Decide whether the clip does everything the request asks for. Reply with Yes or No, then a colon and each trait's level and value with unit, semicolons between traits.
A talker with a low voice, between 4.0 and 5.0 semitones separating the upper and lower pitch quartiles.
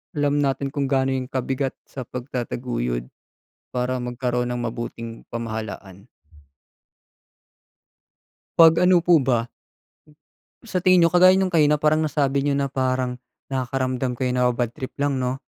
No: low, 130 Hz; average, 2.8 semitones